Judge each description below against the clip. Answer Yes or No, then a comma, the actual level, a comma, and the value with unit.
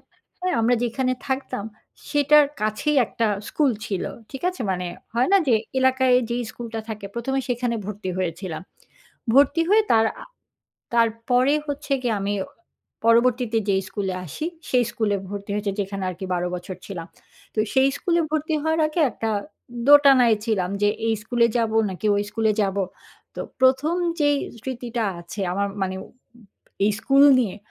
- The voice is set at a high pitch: Yes, high, 235 Hz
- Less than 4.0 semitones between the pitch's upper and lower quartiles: No, average, 4.7 semitones